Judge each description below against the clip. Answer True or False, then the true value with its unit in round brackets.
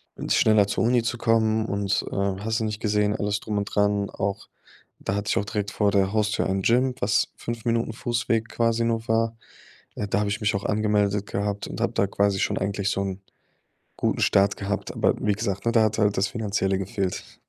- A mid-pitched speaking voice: False (105 Hz)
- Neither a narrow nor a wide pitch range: False (2.0 semitones)